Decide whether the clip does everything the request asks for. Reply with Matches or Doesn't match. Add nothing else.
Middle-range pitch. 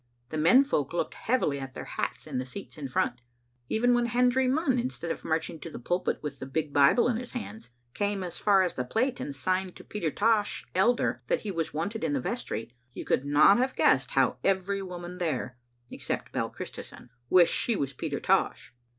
Matches